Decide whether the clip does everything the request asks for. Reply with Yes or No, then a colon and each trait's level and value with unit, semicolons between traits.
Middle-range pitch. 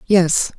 Yes: medium, 180 Hz